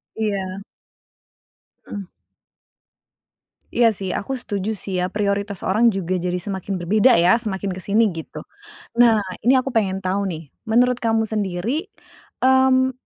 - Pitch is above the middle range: Yes, high, 205 Hz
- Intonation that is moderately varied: Yes, average, 3.6 semitones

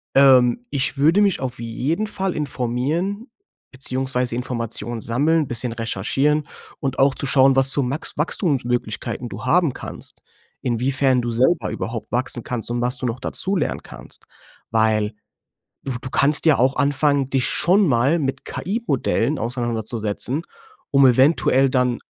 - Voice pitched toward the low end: Yes, low, 130 Hz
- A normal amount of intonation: Yes, average, 3.4 semitones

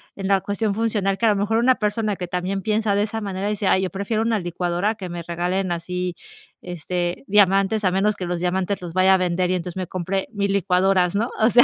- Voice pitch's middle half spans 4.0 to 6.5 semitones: No, narrow, 2.5 semitones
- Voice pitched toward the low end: No, high, 195 Hz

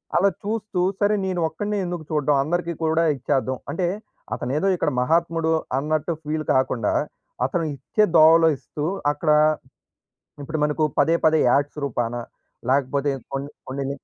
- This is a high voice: No, medium, 155 Hz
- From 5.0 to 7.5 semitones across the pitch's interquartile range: No, average, 3.5 semitones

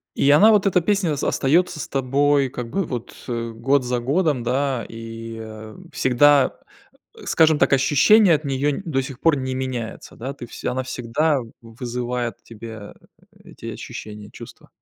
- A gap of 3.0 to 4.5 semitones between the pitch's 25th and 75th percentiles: Yes, average, 3.8 semitones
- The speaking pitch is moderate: No, low, 130 Hz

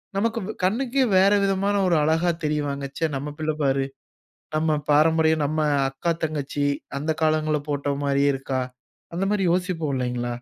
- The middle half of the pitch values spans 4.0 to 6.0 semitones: Yes, average, 4.3 semitones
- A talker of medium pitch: Yes, medium, 155 Hz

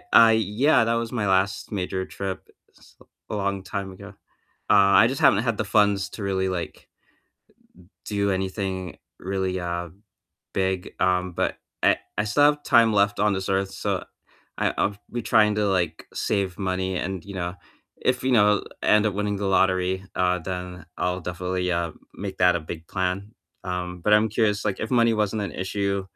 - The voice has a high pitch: No, very low, 95 Hz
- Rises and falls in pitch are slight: Yes, narrow, 2.3 semitones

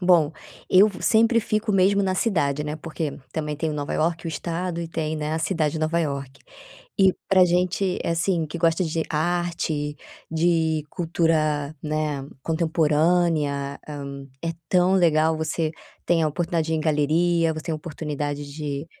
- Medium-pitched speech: Yes, medium, 160 Hz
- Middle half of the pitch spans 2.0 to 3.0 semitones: Yes, narrow, 2.5 semitones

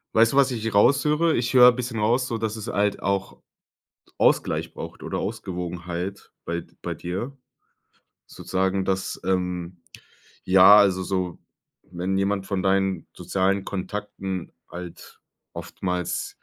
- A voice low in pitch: Yes, very low, 95 Hz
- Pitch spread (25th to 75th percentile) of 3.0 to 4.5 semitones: Yes, average, 3.3 semitones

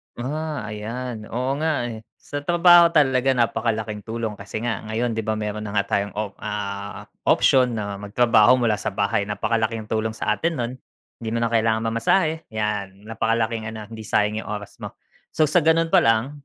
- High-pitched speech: No, low, 115 Hz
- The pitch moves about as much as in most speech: Yes, average, 3.1 semitones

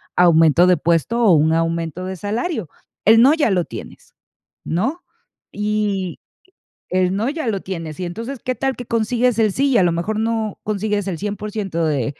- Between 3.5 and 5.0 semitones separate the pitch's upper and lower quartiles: Yes, average, 4.7 semitones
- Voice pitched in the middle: No, high, 205 Hz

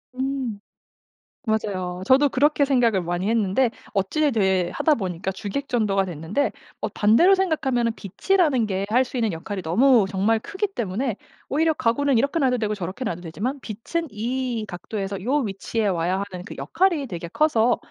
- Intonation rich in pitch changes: Yes, wide, 5.9 semitones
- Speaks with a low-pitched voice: No, high, 225 Hz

